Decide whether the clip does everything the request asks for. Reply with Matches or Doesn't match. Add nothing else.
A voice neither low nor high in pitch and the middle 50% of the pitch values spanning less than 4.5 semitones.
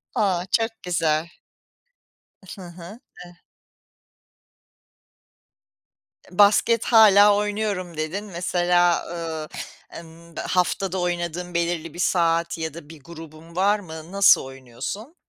Matches